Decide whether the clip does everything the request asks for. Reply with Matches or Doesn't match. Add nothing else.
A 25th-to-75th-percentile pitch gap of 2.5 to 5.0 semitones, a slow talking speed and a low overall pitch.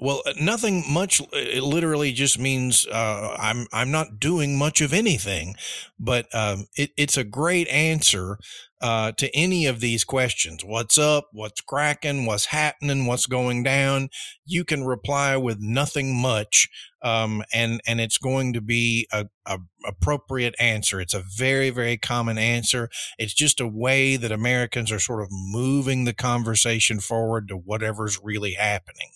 Doesn't match